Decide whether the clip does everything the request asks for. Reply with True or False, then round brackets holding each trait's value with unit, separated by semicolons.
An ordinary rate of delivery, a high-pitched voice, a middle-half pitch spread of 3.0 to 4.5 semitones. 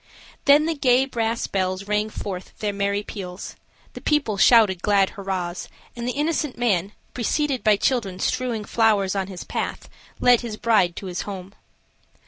True (160 wpm; 210 Hz; 4.1 semitones)